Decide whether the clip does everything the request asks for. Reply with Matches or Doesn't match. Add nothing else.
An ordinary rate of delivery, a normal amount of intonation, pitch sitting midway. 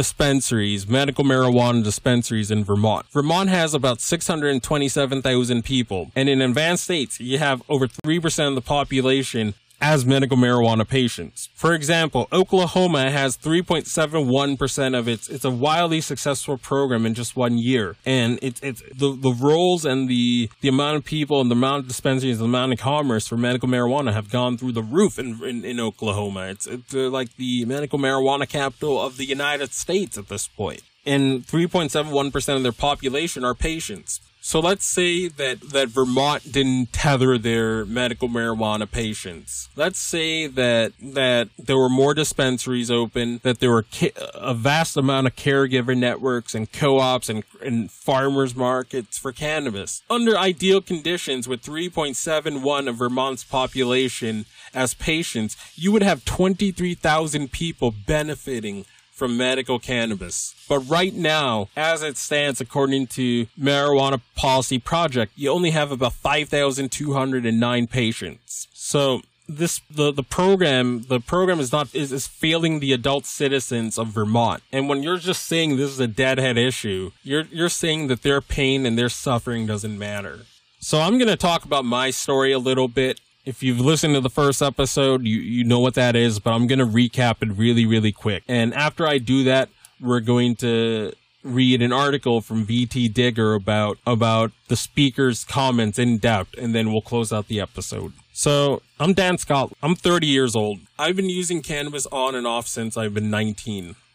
Doesn't match